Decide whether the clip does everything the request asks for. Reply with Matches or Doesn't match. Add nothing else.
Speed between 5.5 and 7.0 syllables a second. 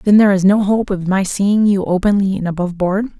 Matches